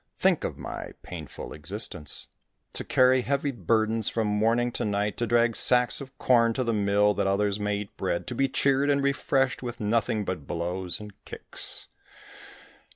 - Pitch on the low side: Yes, low, 110 Hz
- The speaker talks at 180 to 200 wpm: No, average, 170 wpm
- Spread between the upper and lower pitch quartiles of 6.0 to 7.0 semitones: No, average, 3.5 semitones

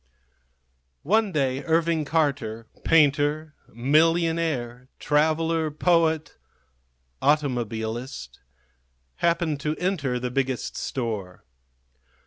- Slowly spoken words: Yes, slow, 75 wpm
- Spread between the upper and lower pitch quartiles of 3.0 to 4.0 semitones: No, average, 4.6 semitones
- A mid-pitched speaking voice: Yes, medium, 150 Hz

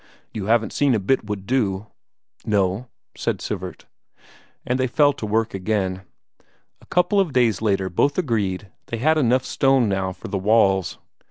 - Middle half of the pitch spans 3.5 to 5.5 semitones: Yes, average, 5.0 semitones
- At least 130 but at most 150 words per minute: No, average, 165 wpm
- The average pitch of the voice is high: No, low, 110 Hz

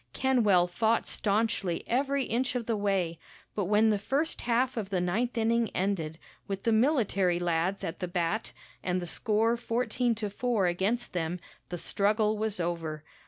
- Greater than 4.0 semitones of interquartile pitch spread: Yes, average, 4.5 semitones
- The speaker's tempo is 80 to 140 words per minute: No, average, 165 wpm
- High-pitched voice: Yes, high, 210 Hz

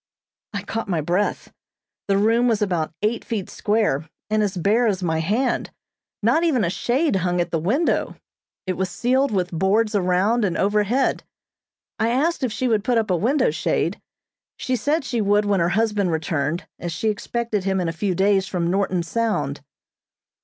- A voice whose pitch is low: No, high, 205 Hz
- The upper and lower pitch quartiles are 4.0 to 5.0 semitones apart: Yes, average, 4.3 semitones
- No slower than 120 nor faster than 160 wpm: No, average, 180 wpm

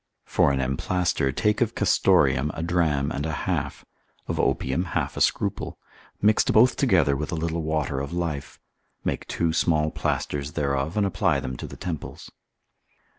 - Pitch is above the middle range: No, very low, 80 Hz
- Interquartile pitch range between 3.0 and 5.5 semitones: Yes, average, 4.0 semitones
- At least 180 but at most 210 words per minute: No, average, 165 wpm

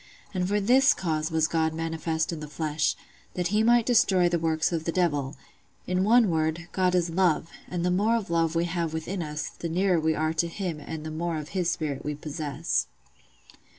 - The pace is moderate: No, fast, 210 wpm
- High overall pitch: No, medium, 165 Hz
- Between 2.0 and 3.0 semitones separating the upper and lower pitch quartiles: Yes, narrow, 2.5 semitones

